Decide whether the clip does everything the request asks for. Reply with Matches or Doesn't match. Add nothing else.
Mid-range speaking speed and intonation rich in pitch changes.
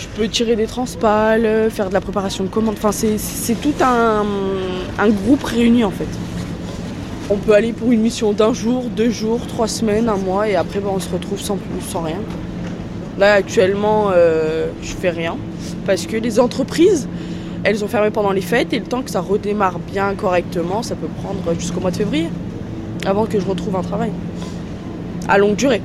Doesn't match